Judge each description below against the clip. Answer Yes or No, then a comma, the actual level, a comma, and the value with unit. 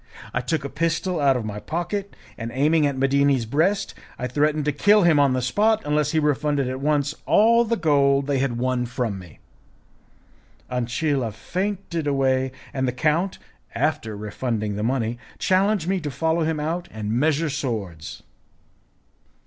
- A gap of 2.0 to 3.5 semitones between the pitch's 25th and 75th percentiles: No, average, 4.5 semitones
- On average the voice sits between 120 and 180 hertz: Yes, medium, 140 Hz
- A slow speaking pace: No, average, 165 wpm